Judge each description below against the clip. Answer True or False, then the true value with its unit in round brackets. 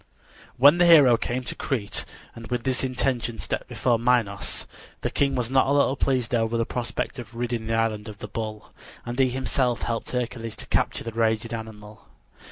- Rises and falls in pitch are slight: True (2.2 semitones)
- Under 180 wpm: False (190 wpm)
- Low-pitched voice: True (120 Hz)